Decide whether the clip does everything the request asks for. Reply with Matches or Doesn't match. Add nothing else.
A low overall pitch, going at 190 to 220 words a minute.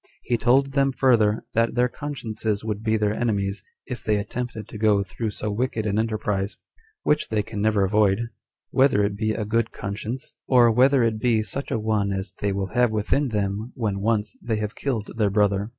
Matches